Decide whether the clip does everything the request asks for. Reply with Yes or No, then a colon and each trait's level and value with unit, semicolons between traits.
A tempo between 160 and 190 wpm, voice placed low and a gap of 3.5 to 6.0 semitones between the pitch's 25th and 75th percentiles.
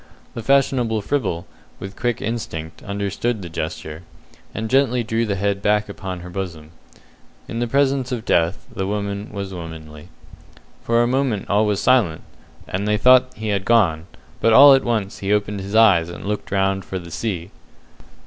Yes: average, 175 wpm; low, 100 Hz; average, 4.0 semitones